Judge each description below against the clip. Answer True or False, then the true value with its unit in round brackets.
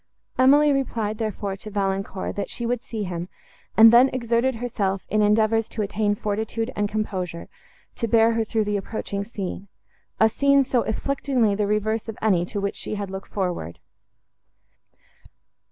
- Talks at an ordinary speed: True (155 wpm)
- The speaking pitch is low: False (215 Hz)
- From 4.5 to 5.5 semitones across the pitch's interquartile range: False (2.5 semitones)